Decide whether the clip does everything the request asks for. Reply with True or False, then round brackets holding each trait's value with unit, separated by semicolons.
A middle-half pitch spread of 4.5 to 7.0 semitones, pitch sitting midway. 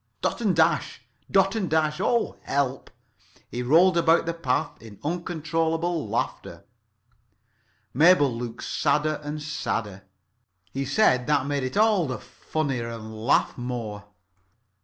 True (5.2 semitones; 150 Hz)